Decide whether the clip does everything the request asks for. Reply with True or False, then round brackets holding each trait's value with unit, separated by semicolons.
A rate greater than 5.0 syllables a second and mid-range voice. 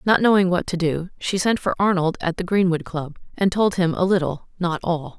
True (5.3 syllables/s; 180 Hz)